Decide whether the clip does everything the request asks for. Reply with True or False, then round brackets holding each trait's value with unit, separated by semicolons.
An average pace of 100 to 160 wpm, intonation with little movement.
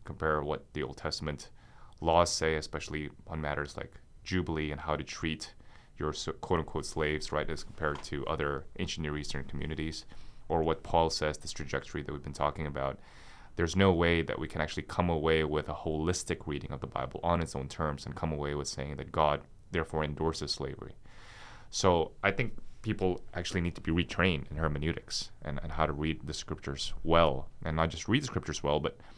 False (200 wpm; 2.2 semitones)